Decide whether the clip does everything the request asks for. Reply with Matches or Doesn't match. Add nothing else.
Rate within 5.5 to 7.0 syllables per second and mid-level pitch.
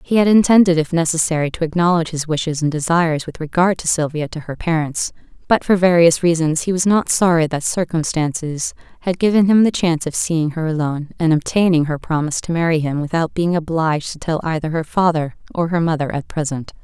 Matches